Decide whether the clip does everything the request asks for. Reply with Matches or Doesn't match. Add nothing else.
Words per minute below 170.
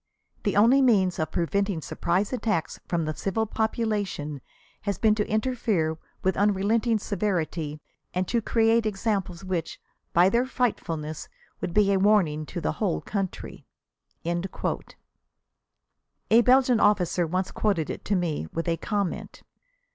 Matches